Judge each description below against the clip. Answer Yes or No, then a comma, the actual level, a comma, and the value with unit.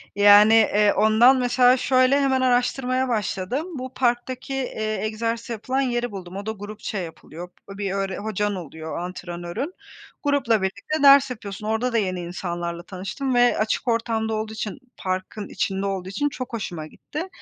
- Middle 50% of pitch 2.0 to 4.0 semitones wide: No, average, 4.6 semitones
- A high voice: Yes, high, 220 Hz